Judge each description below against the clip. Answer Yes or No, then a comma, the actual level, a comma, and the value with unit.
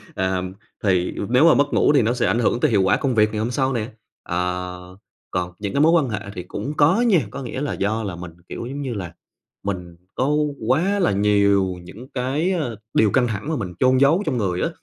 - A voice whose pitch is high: No, low, 115 Hz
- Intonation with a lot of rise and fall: Yes, wide, 6.5 semitones